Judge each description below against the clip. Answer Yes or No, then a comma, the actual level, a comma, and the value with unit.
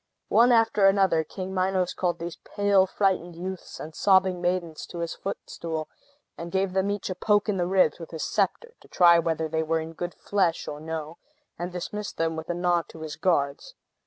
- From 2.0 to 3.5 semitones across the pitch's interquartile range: Yes, average, 2.8 semitones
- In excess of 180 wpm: Yes, average, 195 wpm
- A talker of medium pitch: Yes, medium, 175 Hz